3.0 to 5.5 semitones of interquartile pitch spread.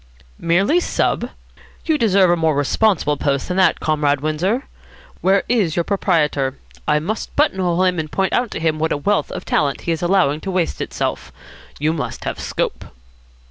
Yes: average, 4.4 semitones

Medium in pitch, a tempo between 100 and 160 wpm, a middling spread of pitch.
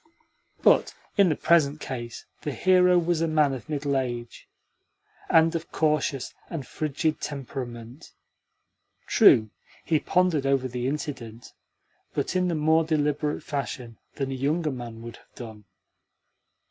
Yes: medium, 145 Hz; slow, 135 wpm; average, 4.1 semitones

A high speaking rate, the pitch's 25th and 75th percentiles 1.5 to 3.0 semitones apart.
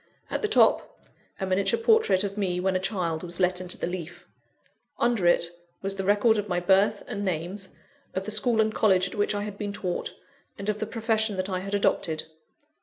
Yes: fast, 210 wpm; narrow, 2.6 semitones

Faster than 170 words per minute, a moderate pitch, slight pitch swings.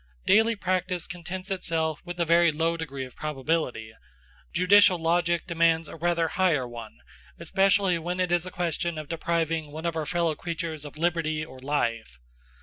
No: average, 165 wpm; medium, 165 Hz; narrow, 2.3 semitones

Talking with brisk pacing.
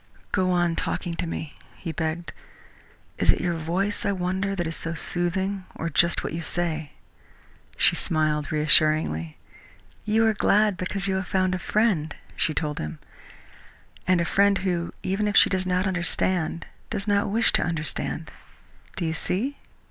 No: average, 165 wpm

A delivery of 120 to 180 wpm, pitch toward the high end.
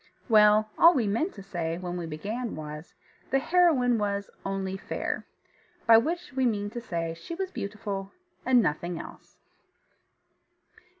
Yes: average, 145 wpm; high, 210 Hz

